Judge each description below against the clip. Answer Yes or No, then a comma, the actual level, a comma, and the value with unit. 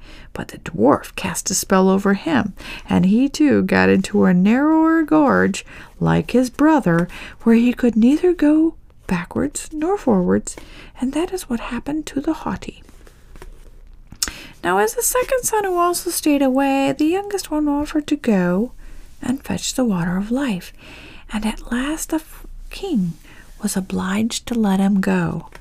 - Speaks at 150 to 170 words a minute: Yes, average, 155 wpm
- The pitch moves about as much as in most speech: No, wide, 7.8 semitones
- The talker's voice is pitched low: No, very high, 255 Hz